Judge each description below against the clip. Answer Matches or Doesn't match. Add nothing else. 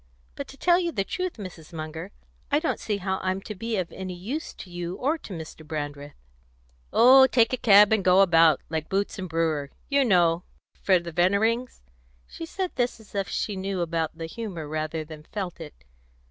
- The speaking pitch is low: Doesn't match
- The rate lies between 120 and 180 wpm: Doesn't match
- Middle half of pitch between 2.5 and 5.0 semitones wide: Doesn't match